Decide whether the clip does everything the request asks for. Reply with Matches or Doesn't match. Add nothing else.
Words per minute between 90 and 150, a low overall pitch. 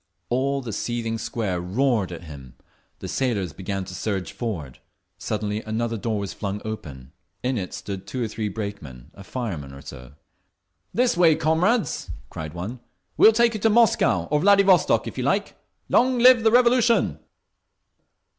Doesn't match